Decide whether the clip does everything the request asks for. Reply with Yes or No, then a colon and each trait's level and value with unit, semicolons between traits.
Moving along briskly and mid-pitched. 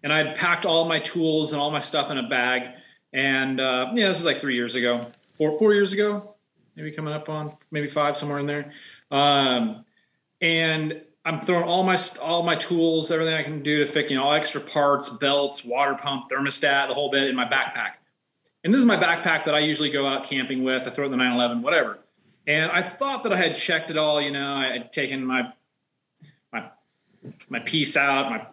Yes: fast, 225 wpm; medium, 150 Hz